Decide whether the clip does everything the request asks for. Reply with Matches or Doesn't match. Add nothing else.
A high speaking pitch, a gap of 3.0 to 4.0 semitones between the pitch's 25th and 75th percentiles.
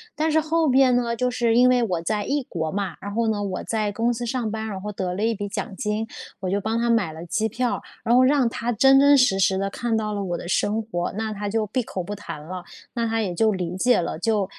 Matches